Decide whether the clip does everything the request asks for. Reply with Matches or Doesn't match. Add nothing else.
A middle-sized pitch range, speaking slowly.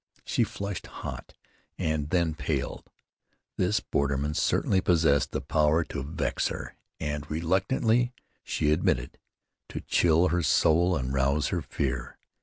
Matches